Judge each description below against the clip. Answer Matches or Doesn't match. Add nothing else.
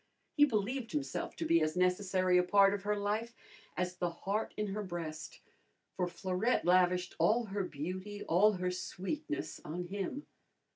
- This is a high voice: Matches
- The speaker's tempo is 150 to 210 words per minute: Matches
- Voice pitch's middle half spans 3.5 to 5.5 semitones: Doesn't match